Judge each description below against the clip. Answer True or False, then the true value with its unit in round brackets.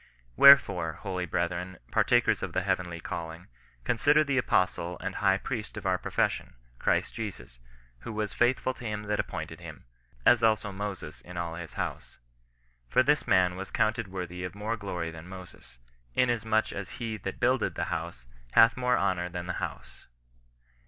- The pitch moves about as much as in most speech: True (4.1 semitones)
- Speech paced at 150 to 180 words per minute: True (170 wpm)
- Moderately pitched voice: False (95 Hz)